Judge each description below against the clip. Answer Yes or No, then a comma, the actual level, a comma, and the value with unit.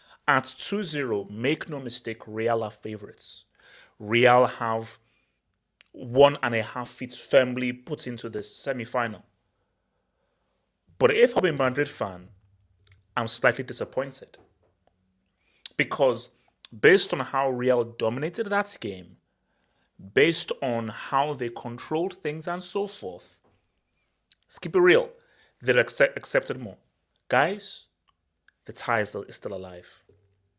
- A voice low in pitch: Yes, low, 120 Hz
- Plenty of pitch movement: Yes, wide, 6.1 semitones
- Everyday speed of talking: No, slow, 115 wpm